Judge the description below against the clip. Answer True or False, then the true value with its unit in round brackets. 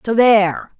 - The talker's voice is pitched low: False (205 Hz)